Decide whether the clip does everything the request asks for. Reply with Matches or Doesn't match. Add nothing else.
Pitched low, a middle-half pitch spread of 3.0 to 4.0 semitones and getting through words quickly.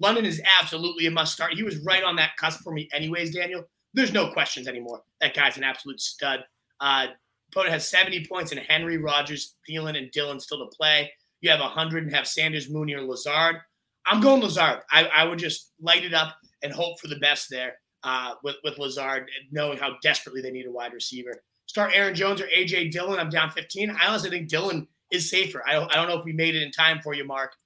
Doesn't match